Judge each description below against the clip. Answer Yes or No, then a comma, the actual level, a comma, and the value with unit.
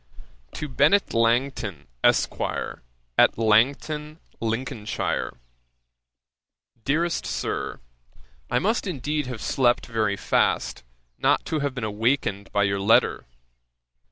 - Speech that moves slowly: Yes, slow, 100 wpm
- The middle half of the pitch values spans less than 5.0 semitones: No, wide, 5.4 semitones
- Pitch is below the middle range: Yes, low, 120 Hz